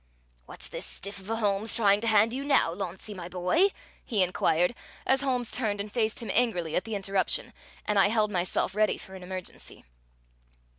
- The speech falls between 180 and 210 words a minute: Yes, average, 190 wpm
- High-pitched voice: Yes, high, 205 Hz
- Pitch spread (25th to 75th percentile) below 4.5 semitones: Yes, average, 3.2 semitones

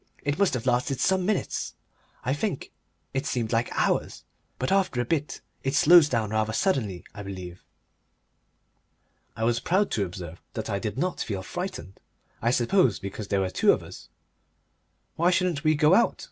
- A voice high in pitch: No, low, 125 Hz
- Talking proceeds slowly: No, average, 175 wpm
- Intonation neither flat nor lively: No, wide, 8.2 semitones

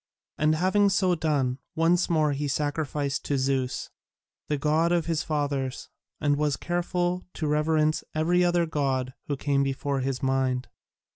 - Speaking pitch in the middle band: Yes, medium, 150 Hz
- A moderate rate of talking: Yes, average, 150 wpm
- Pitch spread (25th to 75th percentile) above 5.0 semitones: No, average, 3.3 semitones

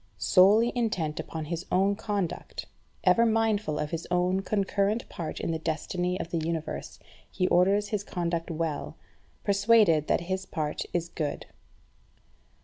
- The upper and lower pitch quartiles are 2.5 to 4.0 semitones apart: Yes, average, 3.7 semitones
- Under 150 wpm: Yes, average, 140 wpm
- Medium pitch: Yes, medium, 180 Hz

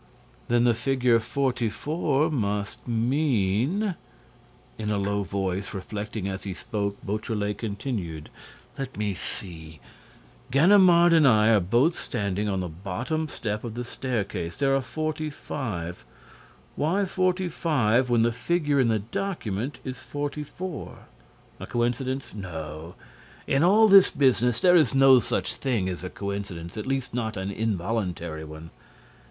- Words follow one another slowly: Yes, slow, 130 wpm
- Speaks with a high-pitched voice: No, low, 115 Hz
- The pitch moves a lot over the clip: Yes, wide, 5.7 semitones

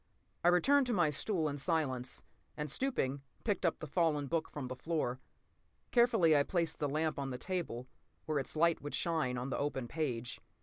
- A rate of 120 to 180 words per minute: No, average, 190 wpm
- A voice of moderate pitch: Yes, medium, 155 Hz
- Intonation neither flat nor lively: Yes, average, 4.1 semitones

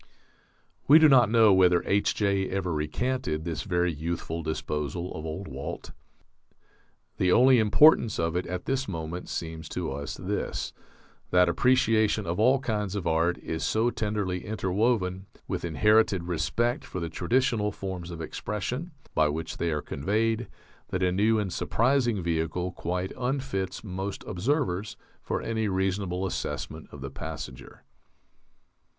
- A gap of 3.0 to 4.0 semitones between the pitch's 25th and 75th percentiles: No, average, 4.6 semitones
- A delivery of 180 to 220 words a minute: No, average, 145 wpm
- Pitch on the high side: No, very low, 95 Hz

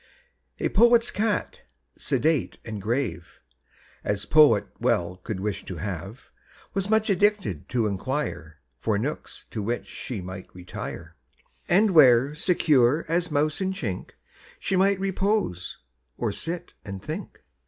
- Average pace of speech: No, slow, 130 wpm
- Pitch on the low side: Yes, low, 130 Hz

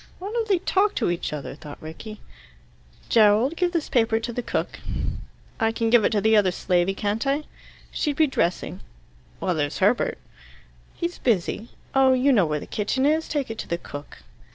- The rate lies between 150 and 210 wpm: Yes, average, 190 wpm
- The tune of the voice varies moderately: No, wide, 7.0 semitones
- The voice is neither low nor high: No, high, 225 Hz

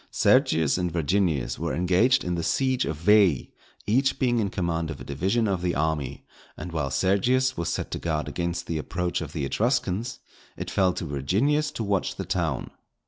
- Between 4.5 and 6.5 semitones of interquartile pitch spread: Yes, wide, 5.6 semitones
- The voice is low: Yes, very low, 90 Hz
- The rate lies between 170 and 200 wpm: Yes, average, 190 wpm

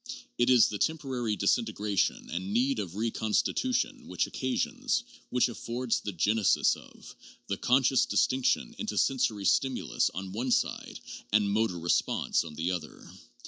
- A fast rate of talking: No, average, 150 wpm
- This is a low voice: Yes, low, 115 Hz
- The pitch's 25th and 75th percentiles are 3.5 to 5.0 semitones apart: Yes, average, 4.6 semitones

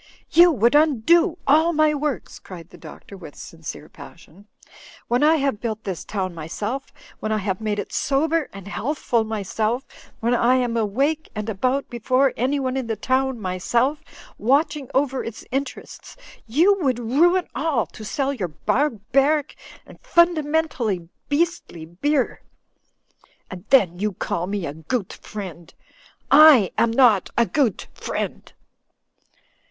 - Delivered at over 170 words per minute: No, average, 145 wpm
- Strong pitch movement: Yes, wide, 6.0 semitones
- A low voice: No, high, 245 Hz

